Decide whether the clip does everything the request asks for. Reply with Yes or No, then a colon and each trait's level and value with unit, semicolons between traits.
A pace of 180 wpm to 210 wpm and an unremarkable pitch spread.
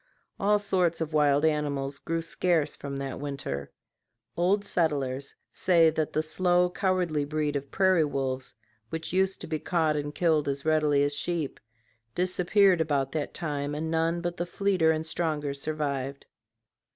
No: average, 155 wpm; average, 3.3 semitones